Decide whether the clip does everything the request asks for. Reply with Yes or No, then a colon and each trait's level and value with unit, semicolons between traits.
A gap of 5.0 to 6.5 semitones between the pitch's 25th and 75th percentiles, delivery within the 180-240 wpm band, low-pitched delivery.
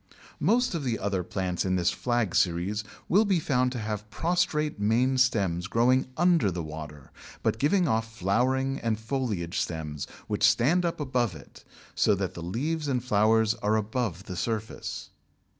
No: wide, 5.6 semitones; average, 165 wpm; low, 110 Hz